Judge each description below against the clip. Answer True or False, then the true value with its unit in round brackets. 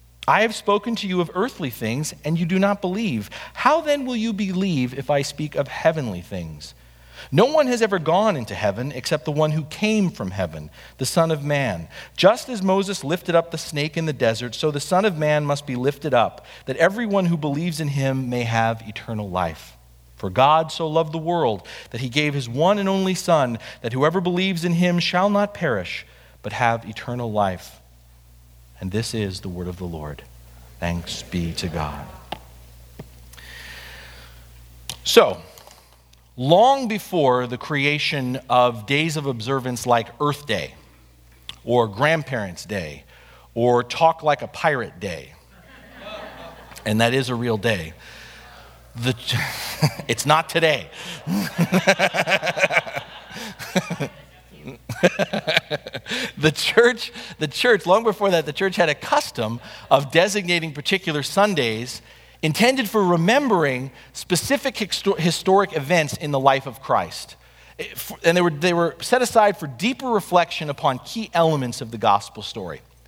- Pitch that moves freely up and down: True (8.8 semitones)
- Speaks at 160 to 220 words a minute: False (150 wpm)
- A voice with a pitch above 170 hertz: False (145 Hz)